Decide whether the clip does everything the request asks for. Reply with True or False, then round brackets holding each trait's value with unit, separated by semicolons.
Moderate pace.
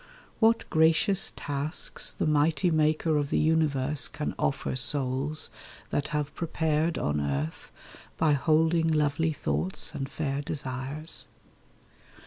False (115 wpm)